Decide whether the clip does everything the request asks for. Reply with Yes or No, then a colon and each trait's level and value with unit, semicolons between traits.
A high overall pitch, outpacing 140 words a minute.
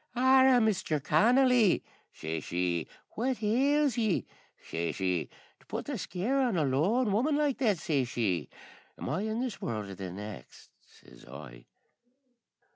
No: high, 195 Hz; slow, 135 wpm